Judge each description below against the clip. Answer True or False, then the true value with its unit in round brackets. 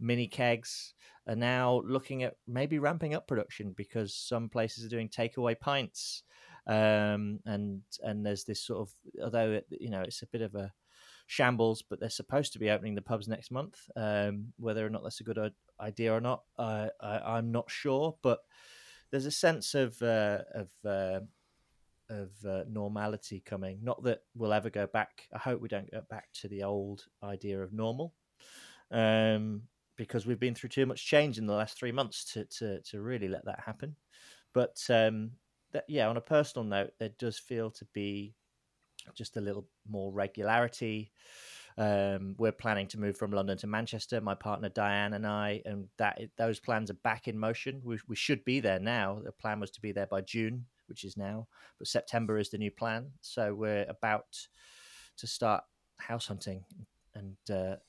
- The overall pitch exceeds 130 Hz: False (110 Hz)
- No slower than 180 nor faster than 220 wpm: True (190 wpm)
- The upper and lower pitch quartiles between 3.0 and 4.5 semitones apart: False (2.6 semitones)